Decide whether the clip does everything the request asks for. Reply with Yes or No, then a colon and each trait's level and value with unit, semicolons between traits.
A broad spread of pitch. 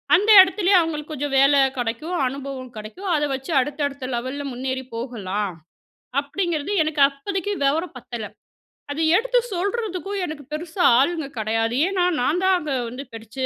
Yes: wide, 5.9 semitones